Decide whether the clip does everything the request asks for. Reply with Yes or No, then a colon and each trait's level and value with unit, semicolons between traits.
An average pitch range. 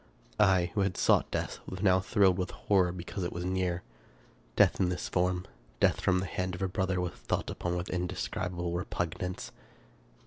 No: narrow, 1.0 semitones